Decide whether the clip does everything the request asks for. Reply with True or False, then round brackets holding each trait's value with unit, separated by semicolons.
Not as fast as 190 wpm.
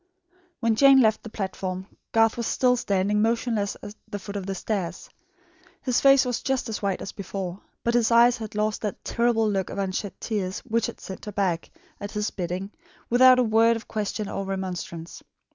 False (195 wpm)